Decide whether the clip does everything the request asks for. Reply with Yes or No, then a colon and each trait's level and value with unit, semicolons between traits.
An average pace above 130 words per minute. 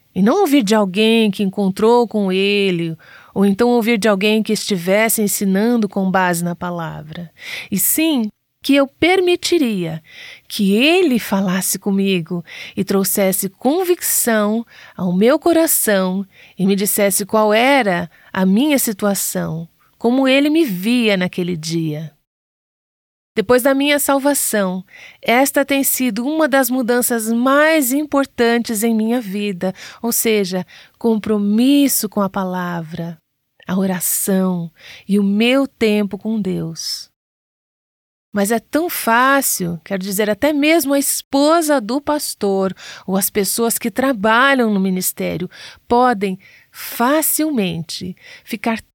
No: average, 125 wpm